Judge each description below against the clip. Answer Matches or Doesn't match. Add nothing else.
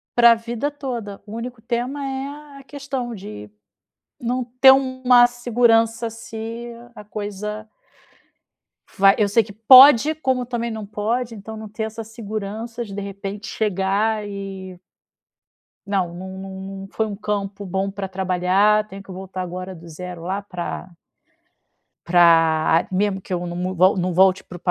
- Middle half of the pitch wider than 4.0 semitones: Doesn't match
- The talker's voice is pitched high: Matches